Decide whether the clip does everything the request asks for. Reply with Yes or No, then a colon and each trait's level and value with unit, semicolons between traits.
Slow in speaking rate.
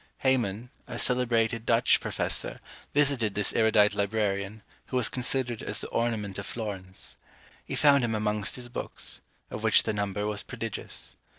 No: average, 155 wpm